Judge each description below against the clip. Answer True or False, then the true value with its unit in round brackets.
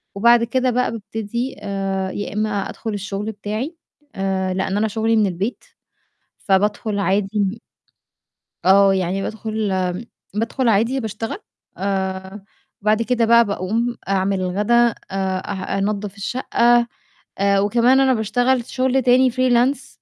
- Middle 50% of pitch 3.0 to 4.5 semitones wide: True (3.3 semitones)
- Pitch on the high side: True (210 Hz)